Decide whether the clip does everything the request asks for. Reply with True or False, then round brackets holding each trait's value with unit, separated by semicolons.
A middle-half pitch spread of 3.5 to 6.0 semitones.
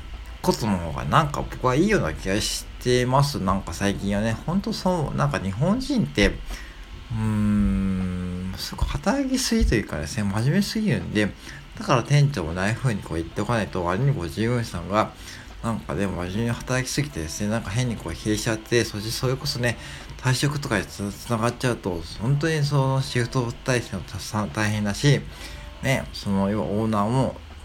True (5.5 semitones)